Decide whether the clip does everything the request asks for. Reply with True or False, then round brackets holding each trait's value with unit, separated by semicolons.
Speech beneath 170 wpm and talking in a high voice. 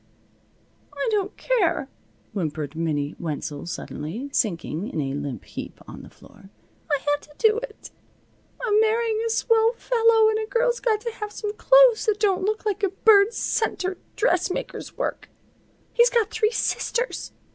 True (155 wpm; 420 Hz)